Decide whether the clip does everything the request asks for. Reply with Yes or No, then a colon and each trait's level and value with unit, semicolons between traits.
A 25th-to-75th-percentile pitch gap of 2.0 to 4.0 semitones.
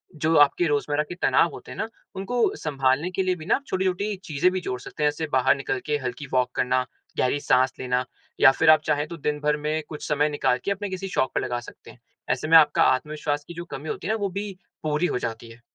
No: average, 4.7 semitones